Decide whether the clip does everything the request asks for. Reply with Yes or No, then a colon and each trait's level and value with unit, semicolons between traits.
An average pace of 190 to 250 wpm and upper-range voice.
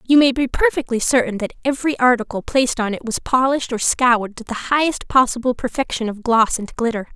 Yes: average, 200 wpm; high, 245 Hz